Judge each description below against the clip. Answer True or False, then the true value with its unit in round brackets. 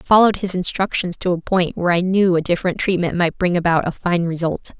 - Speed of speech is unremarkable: False (240 wpm)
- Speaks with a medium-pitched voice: True (180 Hz)